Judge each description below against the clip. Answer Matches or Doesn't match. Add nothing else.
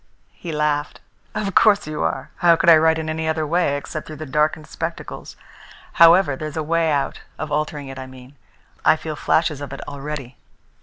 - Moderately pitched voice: Matches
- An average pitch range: Doesn't match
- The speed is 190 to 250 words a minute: Matches